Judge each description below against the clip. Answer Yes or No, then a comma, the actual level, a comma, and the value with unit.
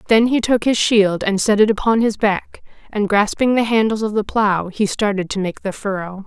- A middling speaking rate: No, fast, 230 wpm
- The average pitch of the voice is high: Yes, high, 210 Hz